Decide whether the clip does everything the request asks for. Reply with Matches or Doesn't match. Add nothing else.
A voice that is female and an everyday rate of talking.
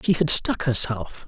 Doesn't match